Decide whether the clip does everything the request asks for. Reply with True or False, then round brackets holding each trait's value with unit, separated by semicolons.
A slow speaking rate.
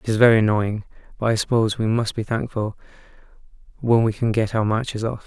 False (205 wpm)